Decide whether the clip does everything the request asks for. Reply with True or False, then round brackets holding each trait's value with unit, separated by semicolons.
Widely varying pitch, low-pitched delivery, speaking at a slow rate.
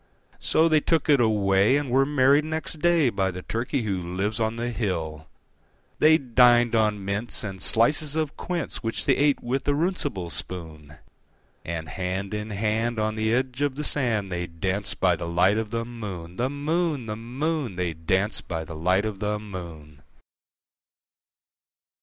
False (6.2 semitones; 110 Hz; 170 wpm)